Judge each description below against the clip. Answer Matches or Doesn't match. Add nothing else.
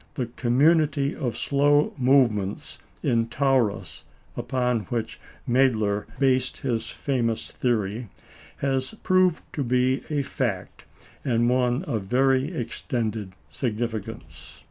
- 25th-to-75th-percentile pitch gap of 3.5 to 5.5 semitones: Doesn't match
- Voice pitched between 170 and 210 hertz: Doesn't match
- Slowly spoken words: Matches